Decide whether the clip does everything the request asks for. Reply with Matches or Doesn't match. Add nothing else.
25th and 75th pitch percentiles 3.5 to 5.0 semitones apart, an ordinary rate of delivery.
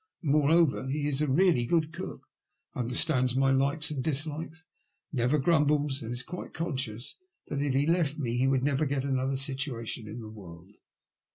Doesn't match